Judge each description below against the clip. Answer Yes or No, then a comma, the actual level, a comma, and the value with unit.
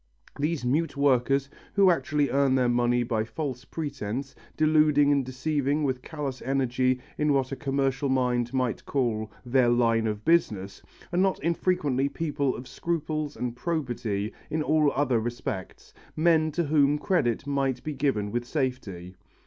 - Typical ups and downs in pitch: Yes, average, 3.6 semitones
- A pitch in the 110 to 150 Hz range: Yes, low, 135 Hz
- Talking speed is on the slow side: No, average, 150 wpm